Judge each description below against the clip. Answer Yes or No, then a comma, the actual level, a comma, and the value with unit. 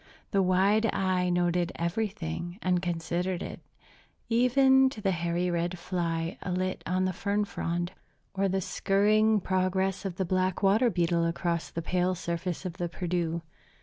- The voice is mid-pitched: Yes, medium, 180 Hz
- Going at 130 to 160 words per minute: Yes, average, 150 wpm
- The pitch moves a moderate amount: No, narrow, 2.1 semitones